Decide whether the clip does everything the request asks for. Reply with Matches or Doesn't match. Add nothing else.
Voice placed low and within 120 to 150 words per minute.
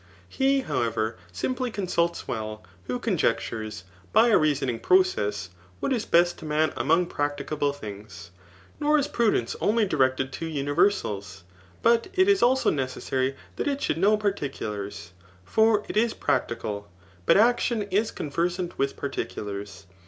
Doesn't match